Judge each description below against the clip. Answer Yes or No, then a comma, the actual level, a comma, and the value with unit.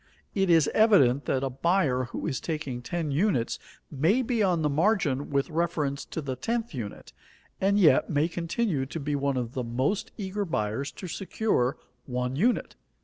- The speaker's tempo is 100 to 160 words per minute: No, average, 175 wpm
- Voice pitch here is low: No, medium, 150 Hz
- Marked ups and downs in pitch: Yes, wide, 6.4 semitones